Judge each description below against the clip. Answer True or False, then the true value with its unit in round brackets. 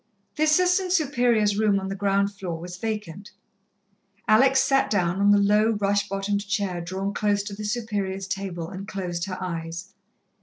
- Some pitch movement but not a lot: False (2.2 semitones)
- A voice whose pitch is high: True (200 Hz)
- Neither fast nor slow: True (165 wpm)